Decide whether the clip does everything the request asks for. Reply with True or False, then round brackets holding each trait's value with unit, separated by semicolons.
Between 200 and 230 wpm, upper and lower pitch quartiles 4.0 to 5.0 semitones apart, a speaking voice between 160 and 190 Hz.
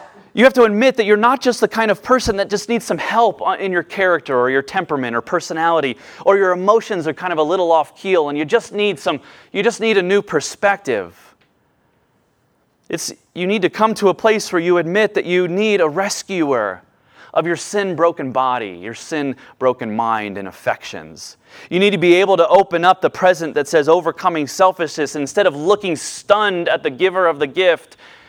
True (205 wpm; 4.3 semitones; 185 Hz)